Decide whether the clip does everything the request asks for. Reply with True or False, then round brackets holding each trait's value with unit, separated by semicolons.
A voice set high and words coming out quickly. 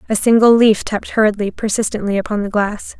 False (210 Hz; 180 wpm)